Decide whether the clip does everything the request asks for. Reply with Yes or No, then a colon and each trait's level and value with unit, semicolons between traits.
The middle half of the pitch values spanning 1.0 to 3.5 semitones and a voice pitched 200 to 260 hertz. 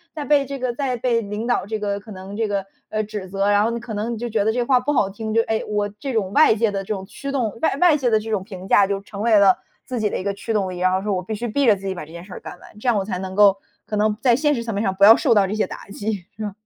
Yes: average, 2.9 semitones; high, 215 Hz